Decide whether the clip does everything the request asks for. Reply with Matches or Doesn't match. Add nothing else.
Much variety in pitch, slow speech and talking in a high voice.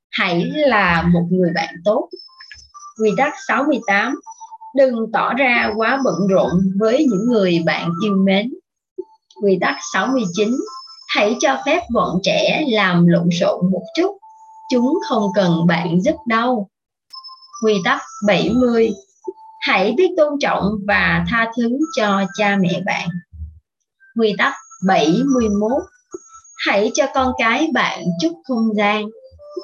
Matches